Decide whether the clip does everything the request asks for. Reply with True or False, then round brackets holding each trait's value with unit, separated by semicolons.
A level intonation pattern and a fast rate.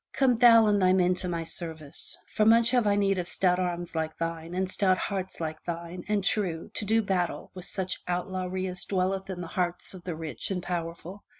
True (2.3 semitones; 220 wpm)